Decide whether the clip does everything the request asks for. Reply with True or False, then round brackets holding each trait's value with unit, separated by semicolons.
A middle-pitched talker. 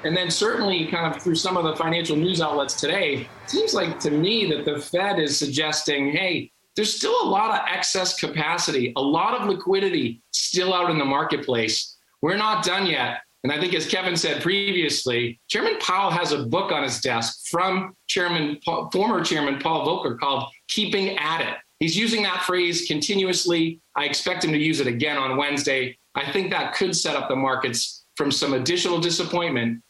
True (165 Hz)